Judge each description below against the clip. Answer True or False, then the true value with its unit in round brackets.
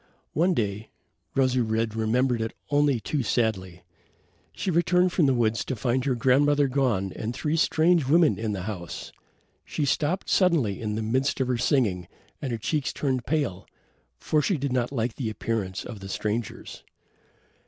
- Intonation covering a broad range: False (4.7 semitones)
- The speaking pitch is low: True (125 Hz)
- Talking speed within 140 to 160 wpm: False (170 wpm)